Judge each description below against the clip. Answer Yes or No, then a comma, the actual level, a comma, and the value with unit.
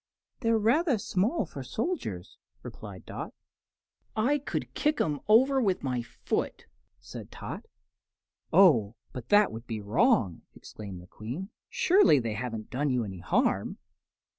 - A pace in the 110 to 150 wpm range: Yes, average, 140 wpm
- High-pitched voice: No, medium, 150 Hz